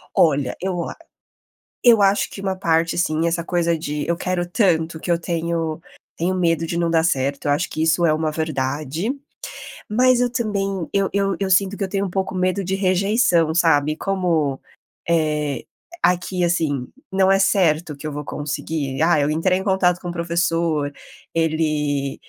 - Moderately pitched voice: Yes, medium, 170 Hz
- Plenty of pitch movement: No, average, 3.4 semitones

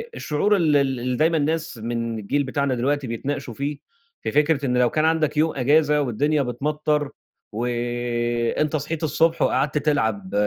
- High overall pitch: No, medium, 140 Hz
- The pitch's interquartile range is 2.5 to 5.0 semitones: Yes, average, 3.8 semitones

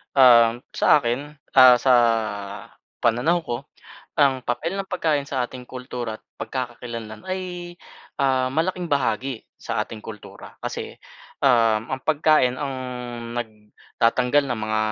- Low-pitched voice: Yes, low, 130 Hz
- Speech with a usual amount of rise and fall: Yes, average, 3.7 semitones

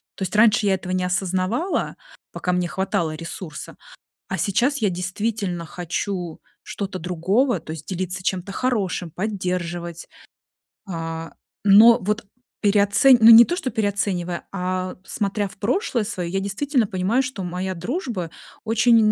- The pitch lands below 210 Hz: Yes, high, 190 Hz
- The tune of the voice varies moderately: Yes, average, 3.5 semitones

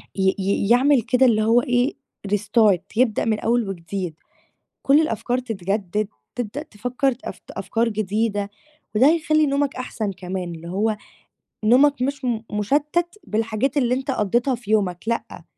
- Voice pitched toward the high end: Yes, high, 225 Hz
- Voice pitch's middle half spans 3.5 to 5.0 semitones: Yes, average, 4.2 semitones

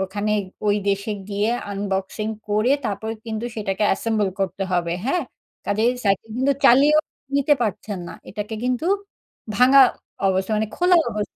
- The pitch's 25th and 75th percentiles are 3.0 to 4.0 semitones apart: Yes, average, 3.5 semitones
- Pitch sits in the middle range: No, high, 210 Hz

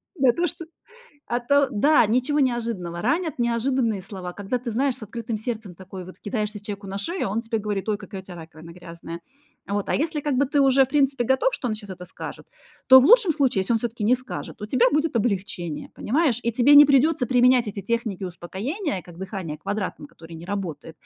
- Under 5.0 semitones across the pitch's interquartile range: No, wide, 5.6 semitones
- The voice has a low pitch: No, high, 230 Hz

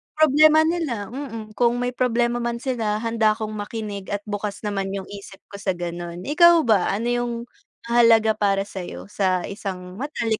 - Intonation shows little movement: No, average, 3.3 semitones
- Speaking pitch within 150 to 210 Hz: No, high, 220 Hz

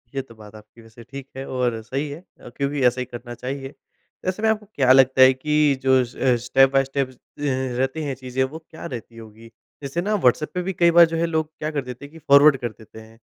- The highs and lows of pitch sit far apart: No, average, 3.6 semitones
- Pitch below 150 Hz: Yes, low, 135 Hz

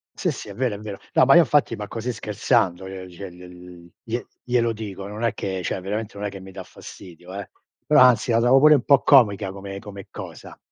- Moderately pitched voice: No, low, 100 Hz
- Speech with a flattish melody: No, average, 3.7 semitones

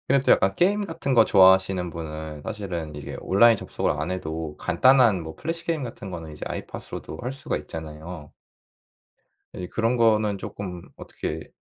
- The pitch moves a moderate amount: No, wide, 6.6 semitones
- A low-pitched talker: Yes, very low, 95 Hz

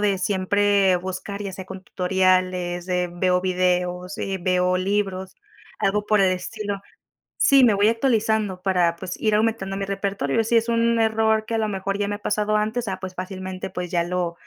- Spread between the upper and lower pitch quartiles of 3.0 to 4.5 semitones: No, narrow, 2.5 semitones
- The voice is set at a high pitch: Yes, high, 195 Hz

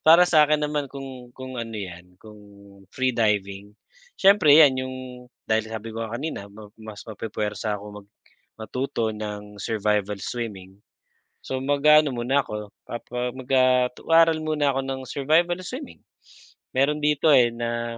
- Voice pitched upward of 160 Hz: No, low, 120 Hz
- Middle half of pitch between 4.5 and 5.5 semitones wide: Yes, average, 5.1 semitones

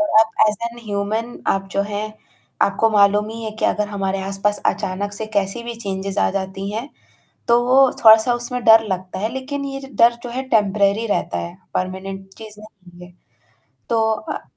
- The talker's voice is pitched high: Yes, high, 210 Hz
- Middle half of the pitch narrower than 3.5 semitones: Yes, average, 2.8 semitones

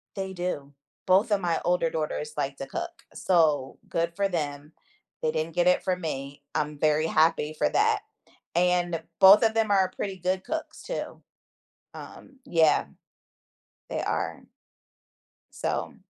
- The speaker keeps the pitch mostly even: No, average, 3.9 semitones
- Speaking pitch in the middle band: Yes, medium, 175 Hz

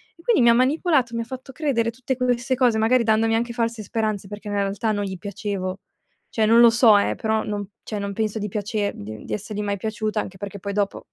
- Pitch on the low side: No, high, 220 Hz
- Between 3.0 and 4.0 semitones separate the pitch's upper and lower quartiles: No, narrow, 2.6 semitones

